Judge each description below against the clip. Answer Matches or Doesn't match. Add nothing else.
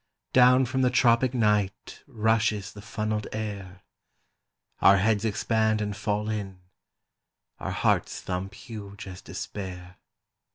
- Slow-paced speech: Matches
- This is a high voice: Doesn't match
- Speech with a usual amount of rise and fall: Doesn't match